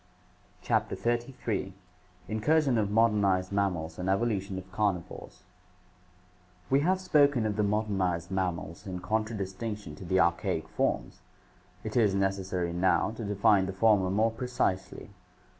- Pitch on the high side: No, low, 100 Hz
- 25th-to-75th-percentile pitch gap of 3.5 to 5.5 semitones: No, average, 3.1 semitones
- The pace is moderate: No, slow, 125 wpm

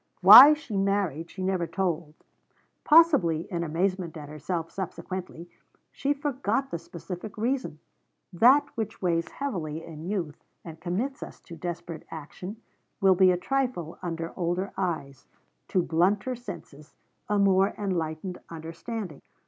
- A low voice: No, medium, 180 Hz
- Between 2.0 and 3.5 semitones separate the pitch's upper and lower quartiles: No, average, 4.1 semitones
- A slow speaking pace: Yes, slow, 130 wpm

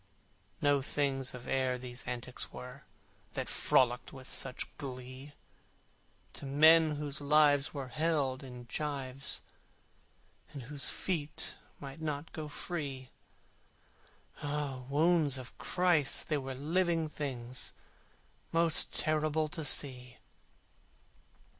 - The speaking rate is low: Yes, slow, 110 wpm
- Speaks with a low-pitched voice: No, medium, 145 Hz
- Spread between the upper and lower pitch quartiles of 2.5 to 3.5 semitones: Yes, average, 2.9 semitones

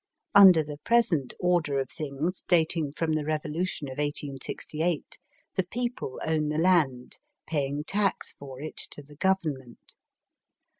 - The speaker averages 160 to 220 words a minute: No, slow, 135 wpm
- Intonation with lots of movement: No, average, 3.8 semitones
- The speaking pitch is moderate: Yes, medium, 155 Hz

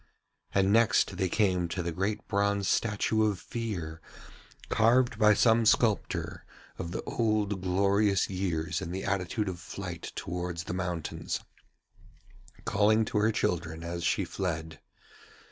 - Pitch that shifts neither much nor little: Yes, average, 3.5 semitones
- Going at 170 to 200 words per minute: No, slow, 135 wpm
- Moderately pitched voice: No, very low, 95 Hz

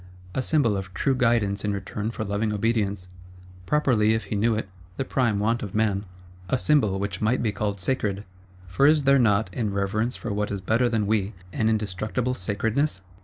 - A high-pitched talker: No, low, 105 Hz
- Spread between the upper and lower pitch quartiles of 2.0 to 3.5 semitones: Yes, average, 2.8 semitones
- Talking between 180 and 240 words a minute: Yes, average, 190 wpm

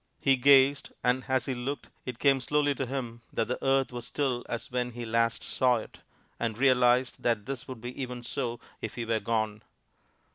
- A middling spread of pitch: No, narrow, 2.2 semitones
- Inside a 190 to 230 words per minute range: Yes, average, 195 wpm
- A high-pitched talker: No, low, 125 Hz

